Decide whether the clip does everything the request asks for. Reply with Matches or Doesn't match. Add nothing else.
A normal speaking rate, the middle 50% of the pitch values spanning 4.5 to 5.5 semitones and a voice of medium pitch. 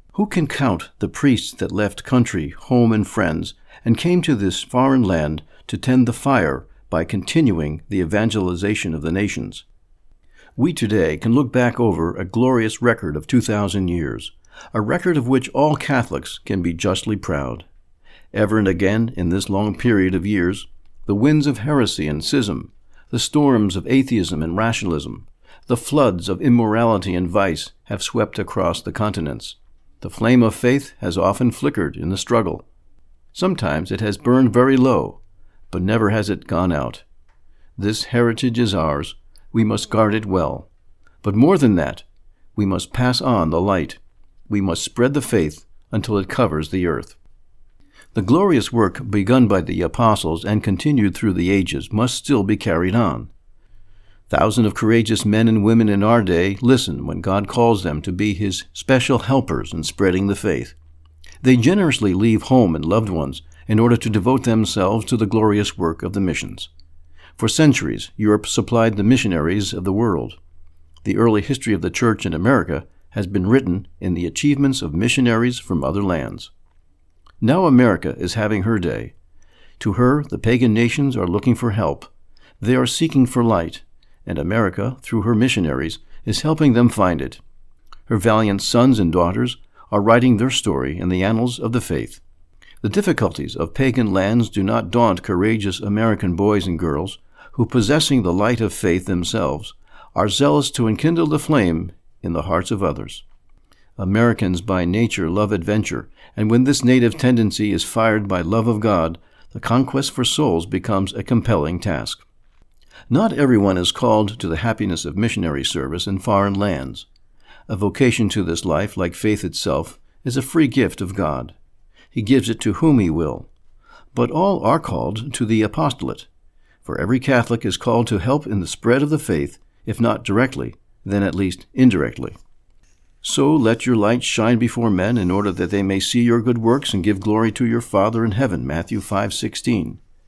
Doesn't match